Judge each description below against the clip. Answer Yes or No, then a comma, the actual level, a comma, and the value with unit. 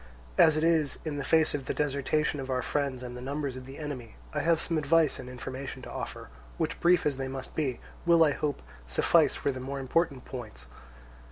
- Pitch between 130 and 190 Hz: Yes, medium, 140 Hz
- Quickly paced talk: Yes, fast, 215 wpm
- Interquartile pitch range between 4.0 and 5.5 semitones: No, average, 3.0 semitones